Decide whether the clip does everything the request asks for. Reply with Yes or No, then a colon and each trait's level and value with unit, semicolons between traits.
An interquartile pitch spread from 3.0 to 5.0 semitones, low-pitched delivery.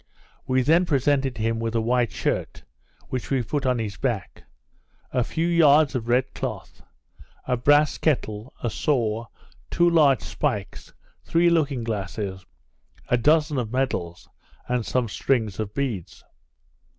Yes: average, 4.3 semitones; low, 125 Hz